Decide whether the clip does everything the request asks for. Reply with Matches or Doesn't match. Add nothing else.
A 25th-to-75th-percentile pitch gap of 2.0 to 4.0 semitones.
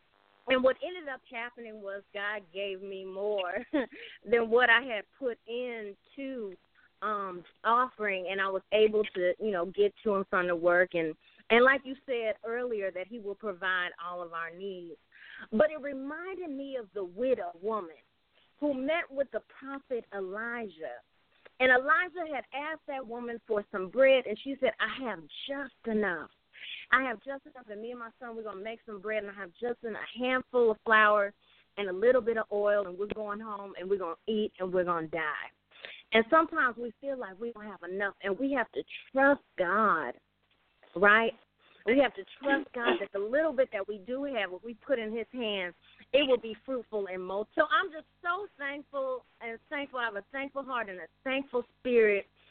Doesn't match